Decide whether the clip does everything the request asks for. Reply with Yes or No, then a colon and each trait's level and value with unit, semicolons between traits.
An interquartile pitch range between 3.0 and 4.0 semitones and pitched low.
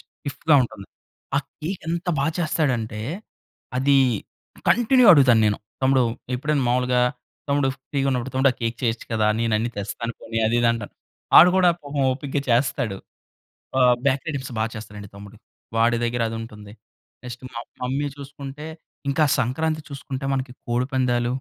Yes: average, 3.5 semitones; low, 130 Hz